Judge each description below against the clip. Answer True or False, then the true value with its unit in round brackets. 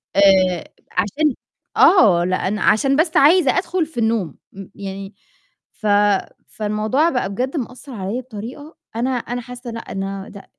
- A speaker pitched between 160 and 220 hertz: False (230 Hz)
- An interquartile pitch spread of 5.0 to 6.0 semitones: True (5.4 semitones)